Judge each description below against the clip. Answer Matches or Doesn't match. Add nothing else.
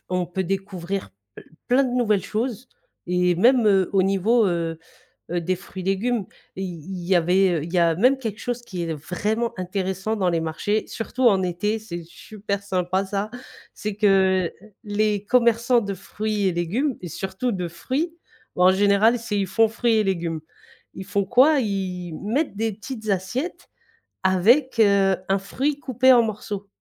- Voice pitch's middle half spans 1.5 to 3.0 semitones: Doesn't match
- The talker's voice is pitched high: Matches